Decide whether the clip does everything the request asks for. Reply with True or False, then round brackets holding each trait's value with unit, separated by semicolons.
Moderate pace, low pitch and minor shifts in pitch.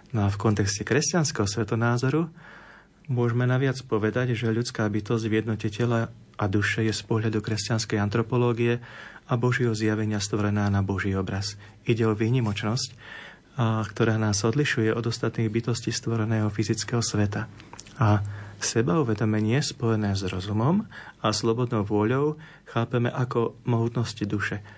True (130 wpm; 115 Hz; 2.2 semitones)